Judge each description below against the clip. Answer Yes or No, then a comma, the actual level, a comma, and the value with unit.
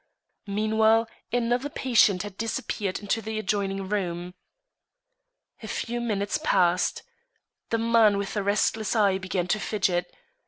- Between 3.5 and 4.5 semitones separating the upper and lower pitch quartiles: No, average, 2.7 semitones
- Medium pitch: No, high, 210 Hz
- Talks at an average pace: No, slow, 125 wpm